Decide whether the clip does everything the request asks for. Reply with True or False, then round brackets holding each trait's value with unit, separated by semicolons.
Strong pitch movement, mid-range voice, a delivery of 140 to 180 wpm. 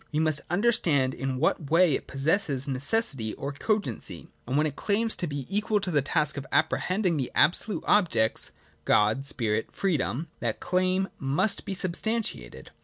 True (6.1 semitones; 155 Hz; 170 wpm)